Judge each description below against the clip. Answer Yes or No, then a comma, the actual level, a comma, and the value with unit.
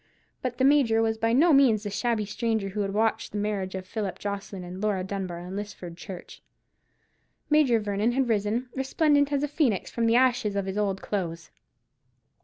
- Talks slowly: No, average, 190 wpm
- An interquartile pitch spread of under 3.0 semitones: No, average, 3.9 semitones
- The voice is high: Yes, high, 215 Hz